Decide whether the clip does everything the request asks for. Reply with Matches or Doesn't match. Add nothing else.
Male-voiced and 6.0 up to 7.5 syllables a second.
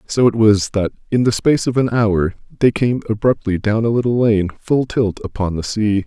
Doesn't match